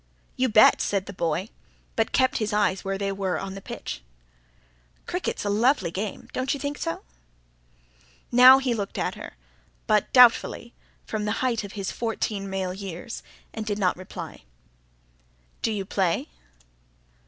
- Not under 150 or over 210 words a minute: Yes, average, 155 wpm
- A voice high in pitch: Yes, high, 210 Hz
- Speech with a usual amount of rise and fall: Yes, average, 3.5 semitones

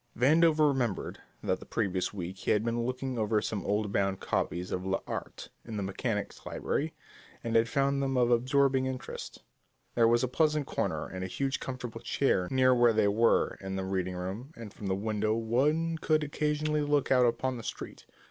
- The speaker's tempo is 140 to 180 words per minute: No, average, 190 wpm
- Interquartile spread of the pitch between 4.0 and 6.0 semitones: Yes, average, 4.9 semitones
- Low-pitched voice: Yes, low, 120 Hz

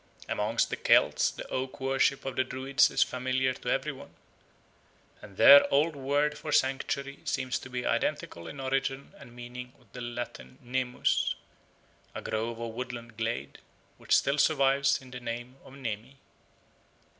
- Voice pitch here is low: Yes, low, 130 Hz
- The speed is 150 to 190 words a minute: Yes, average, 155 wpm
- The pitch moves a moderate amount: No, narrow, 2.1 semitones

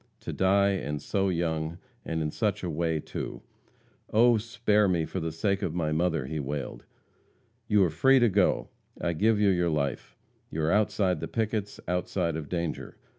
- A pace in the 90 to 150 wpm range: No, average, 185 wpm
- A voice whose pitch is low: Yes, very low, 90 Hz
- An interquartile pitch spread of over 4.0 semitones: Yes, average, 4.4 semitones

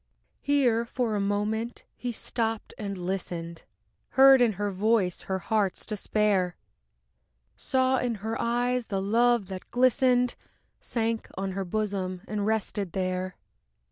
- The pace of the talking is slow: Yes, slow, 130 wpm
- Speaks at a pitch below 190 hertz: No, high, 215 Hz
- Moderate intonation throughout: Yes, average, 3.7 semitones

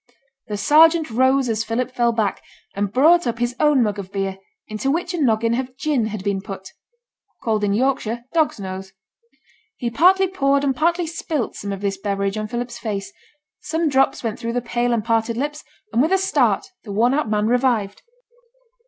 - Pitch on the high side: Yes, high, 235 Hz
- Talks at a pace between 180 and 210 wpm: Yes, average, 190 wpm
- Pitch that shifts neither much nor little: Yes, average, 4.8 semitones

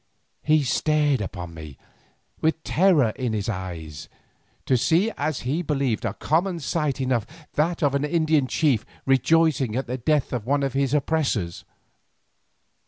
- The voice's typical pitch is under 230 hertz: Yes, medium, 140 Hz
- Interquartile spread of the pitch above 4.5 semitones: Yes, average, 4.9 semitones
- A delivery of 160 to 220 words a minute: No, average, 150 wpm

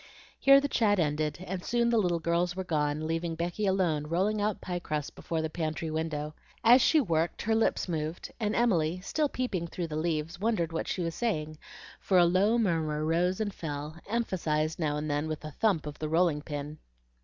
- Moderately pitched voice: Yes, medium, 170 Hz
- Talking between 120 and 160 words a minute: No, average, 200 wpm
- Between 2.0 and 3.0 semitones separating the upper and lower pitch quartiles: No, average, 4.2 semitones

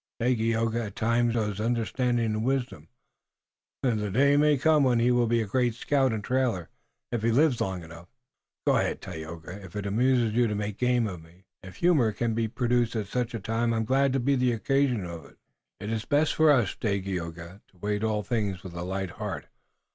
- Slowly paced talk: No, average, 200 wpm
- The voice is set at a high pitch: No, low, 115 Hz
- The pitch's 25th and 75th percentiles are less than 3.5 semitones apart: No, average, 3.8 semitones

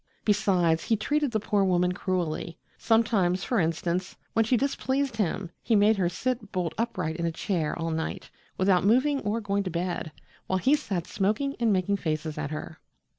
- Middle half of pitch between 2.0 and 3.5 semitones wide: No, average, 4.6 semitones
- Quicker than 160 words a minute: Yes, average, 180 wpm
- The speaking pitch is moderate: No, high, 195 Hz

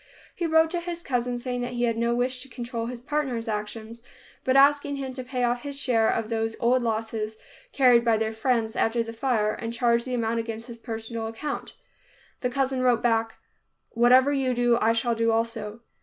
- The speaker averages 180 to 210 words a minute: Yes, average, 200 wpm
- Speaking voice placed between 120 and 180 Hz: No, high, 240 Hz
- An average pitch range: No, narrow, 2.1 semitones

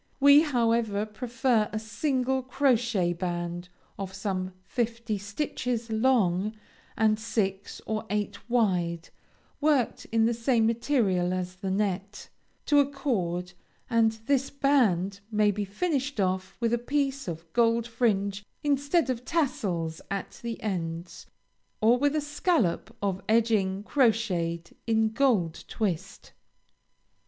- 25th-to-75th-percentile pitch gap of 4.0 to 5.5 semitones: Yes, average, 4.7 semitones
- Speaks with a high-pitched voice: Yes, high, 220 Hz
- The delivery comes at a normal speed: No, slow, 125 wpm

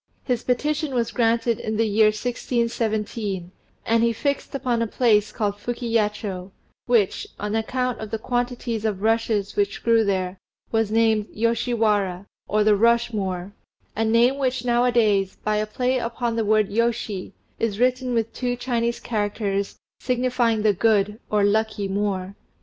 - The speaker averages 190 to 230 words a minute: No, average, 160 wpm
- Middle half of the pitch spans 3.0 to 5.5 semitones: No, narrow, 2.4 semitones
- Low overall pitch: No, high, 225 Hz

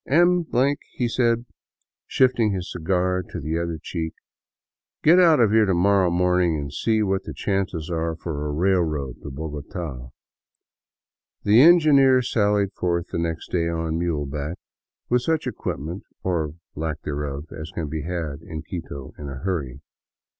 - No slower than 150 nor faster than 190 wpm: Yes, average, 160 wpm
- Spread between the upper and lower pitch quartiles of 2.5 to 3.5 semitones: No, average, 4.9 semitones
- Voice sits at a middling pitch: No, very low, 85 Hz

